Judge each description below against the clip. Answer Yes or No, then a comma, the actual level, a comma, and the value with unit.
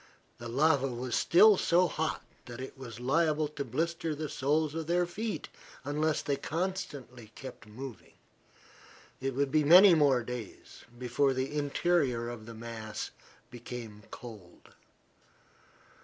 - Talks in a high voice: No, medium, 140 Hz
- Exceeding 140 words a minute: No, slow, 135 wpm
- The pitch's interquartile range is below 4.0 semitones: No, average, 4.7 semitones